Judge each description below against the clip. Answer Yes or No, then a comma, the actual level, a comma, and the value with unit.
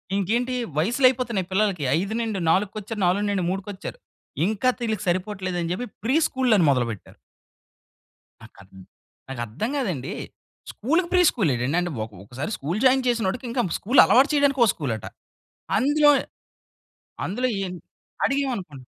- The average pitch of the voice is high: Yes, high, 205 Hz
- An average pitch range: No, wide, 6.4 semitones